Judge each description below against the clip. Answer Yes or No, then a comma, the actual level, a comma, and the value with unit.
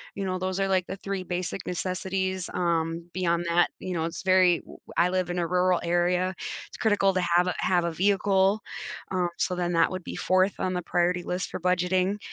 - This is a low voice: No, medium, 180 Hz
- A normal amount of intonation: No, narrow, 1.2 semitones